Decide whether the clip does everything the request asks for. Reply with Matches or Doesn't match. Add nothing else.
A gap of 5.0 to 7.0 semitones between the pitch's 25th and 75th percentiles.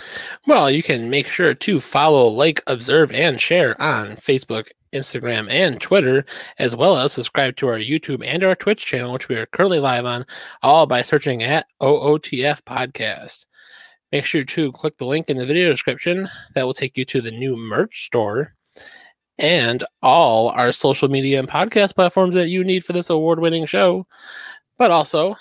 Matches